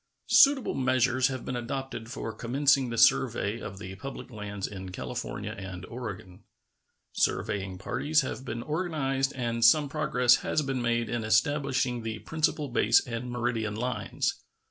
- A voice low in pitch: Yes, low, 120 Hz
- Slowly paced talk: No, average, 145 wpm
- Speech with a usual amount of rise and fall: Yes, average, 3.4 semitones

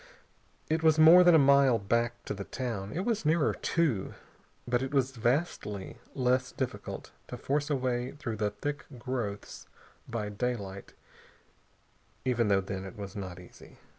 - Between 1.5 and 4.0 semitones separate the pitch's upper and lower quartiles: No, wide, 5.5 semitones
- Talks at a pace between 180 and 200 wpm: No, average, 160 wpm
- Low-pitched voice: Yes, low, 125 Hz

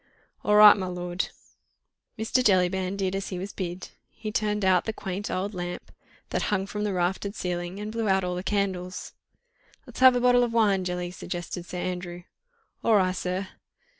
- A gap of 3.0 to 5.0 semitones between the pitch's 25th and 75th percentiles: No, narrow, 2.6 semitones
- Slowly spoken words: No, average, 180 wpm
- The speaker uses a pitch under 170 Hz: No, high, 190 Hz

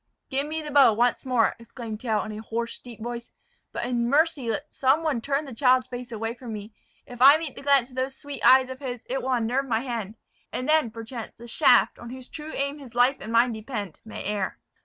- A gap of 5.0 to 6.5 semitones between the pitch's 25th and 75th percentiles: No, average, 3.0 semitones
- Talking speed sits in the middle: No, fast, 235 wpm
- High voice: Yes, high, 245 Hz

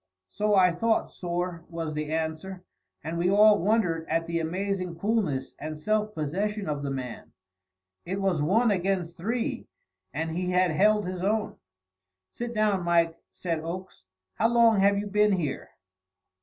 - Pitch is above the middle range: No, medium, 180 Hz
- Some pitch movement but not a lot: Yes, average, 4.2 semitones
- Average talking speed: Yes, average, 155 wpm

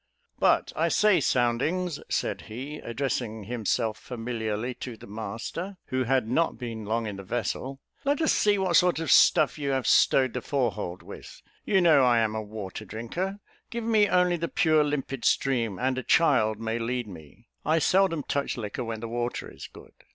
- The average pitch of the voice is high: No, low, 125 Hz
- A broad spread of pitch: Yes, wide, 6.2 semitones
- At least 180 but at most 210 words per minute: Yes, average, 190 wpm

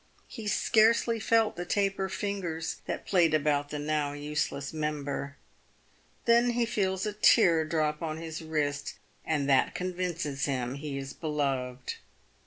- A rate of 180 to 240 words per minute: No, average, 140 wpm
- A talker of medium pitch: Yes, medium, 155 Hz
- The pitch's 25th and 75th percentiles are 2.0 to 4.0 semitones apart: No, average, 4.9 semitones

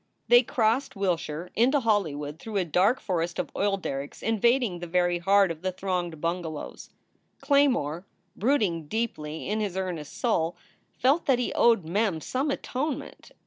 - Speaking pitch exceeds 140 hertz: Yes, high, 190 Hz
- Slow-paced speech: No, average, 150 wpm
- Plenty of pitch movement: Yes, wide, 5.7 semitones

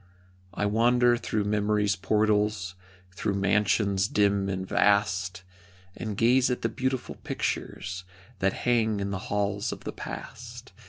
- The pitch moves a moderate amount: No, narrow, 1.8 semitones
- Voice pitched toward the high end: No, low, 105 Hz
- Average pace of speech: No, slow, 130 wpm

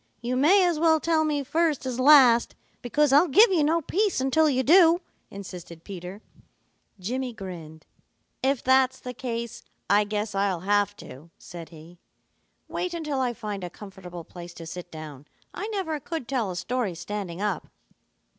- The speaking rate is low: No, average, 165 wpm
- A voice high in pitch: Yes, high, 240 Hz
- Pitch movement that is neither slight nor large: No, wide, 8.4 semitones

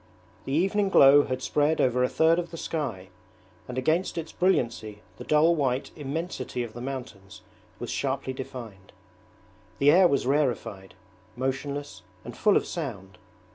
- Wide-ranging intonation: No, average, 4.8 semitones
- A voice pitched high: No, low, 135 Hz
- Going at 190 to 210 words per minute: No, average, 150 wpm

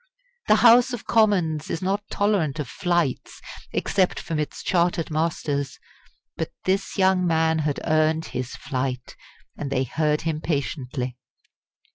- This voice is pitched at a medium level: Yes, medium, 160 Hz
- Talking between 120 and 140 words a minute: Yes, slow, 135 wpm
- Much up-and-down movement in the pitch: No, average, 4.6 semitones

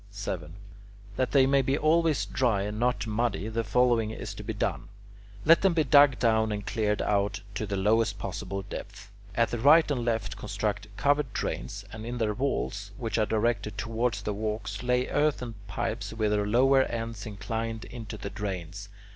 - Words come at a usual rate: Yes, average, 180 wpm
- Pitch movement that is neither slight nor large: Yes, average, 3.2 semitones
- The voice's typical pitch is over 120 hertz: No, low, 110 Hz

